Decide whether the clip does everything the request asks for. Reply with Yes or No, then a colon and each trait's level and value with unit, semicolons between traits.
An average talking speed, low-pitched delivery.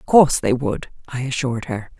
No: fast, 210 wpm; low, 130 Hz